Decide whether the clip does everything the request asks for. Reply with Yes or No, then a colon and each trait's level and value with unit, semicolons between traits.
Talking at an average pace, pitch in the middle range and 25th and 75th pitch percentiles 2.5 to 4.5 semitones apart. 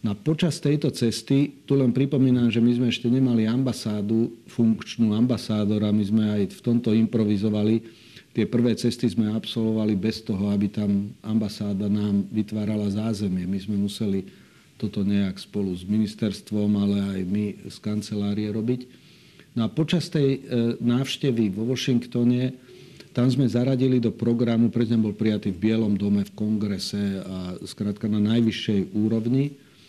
No: average, 150 wpm; low, 110 Hz; average, 2.8 semitones